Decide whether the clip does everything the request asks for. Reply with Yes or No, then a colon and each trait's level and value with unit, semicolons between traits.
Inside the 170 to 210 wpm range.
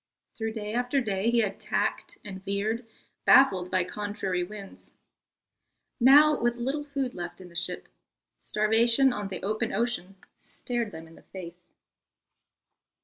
No: average, 145 wpm